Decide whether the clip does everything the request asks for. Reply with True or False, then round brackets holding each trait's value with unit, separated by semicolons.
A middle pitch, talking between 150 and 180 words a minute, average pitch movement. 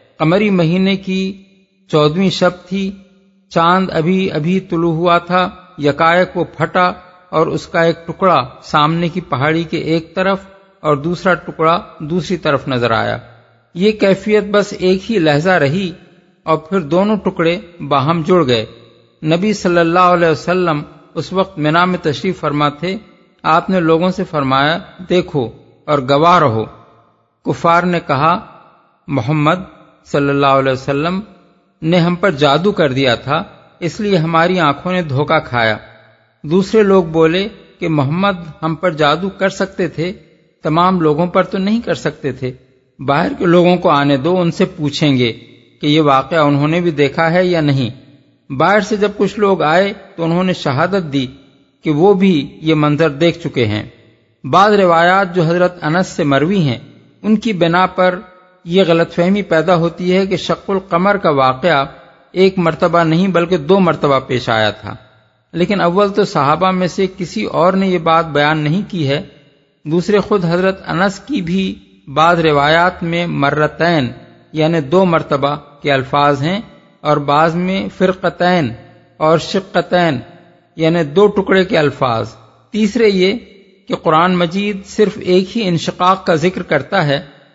True (170 Hz; 160 wpm; 4.0 semitones)